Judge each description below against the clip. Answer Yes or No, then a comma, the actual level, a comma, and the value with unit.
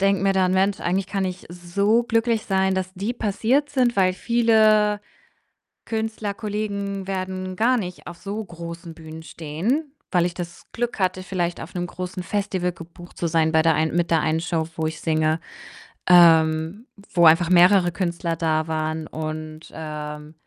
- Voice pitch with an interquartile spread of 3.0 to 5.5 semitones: Yes, average, 3.6 semitones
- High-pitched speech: No, medium, 180 Hz